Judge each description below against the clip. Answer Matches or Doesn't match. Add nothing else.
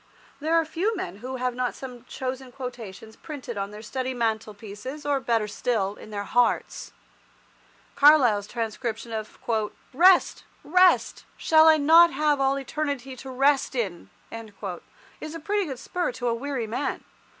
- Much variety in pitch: Doesn't match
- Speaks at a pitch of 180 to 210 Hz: Doesn't match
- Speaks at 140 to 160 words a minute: Matches